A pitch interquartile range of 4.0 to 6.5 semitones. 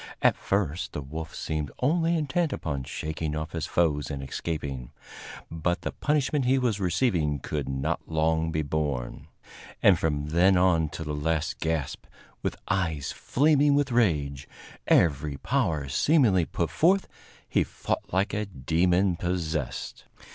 Yes: average, 5.0 semitones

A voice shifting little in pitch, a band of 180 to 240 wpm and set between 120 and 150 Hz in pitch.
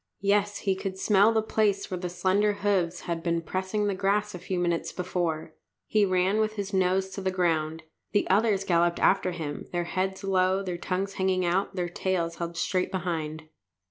No: narrow, 2.2 semitones; average, 195 wpm; medium, 185 Hz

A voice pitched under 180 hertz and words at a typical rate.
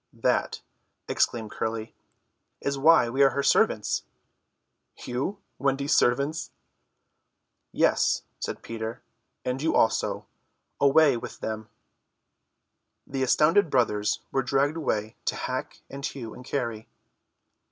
No: low, 135 Hz; slow, 110 wpm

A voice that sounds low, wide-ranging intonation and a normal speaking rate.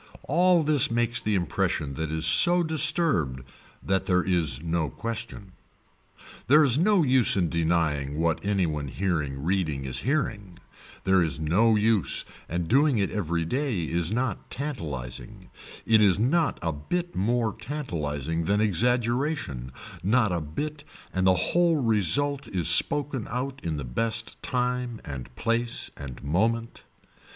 Yes: low, 105 Hz; wide, 7.8 semitones; average, 145 wpm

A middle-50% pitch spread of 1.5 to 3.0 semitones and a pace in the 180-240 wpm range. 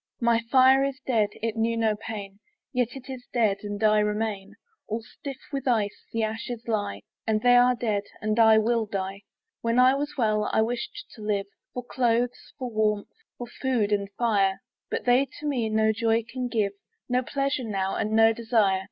Yes: narrow, 2.6 semitones; average, 190 wpm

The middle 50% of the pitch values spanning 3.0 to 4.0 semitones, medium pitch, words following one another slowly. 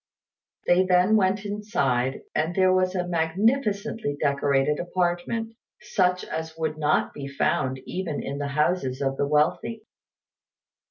No: average, 4.9 semitones; medium, 175 Hz; slow, 130 wpm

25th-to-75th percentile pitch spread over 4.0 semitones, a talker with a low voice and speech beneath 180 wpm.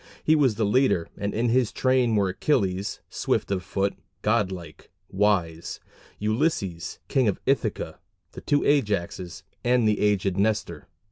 Yes: average, 4.5 semitones; low, 105 Hz; average, 145 wpm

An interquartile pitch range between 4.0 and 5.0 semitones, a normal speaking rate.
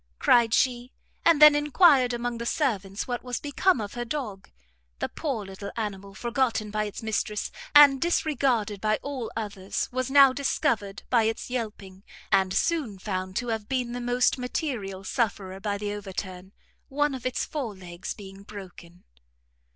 Yes: average, 4.6 semitones; average, 160 wpm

